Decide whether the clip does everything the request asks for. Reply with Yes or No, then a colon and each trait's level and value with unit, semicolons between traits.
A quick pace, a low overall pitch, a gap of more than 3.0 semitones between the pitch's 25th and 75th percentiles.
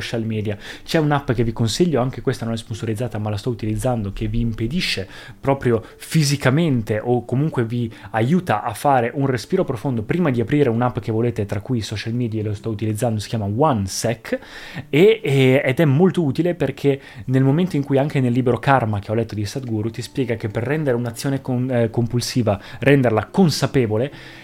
Yes: fast, 185 wpm; low, 120 Hz; average, 3.6 semitones